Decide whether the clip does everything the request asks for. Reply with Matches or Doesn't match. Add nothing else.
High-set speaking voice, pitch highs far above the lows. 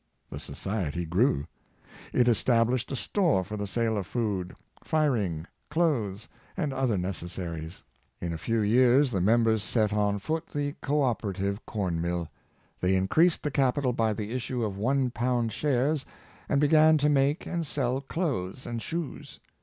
Doesn't match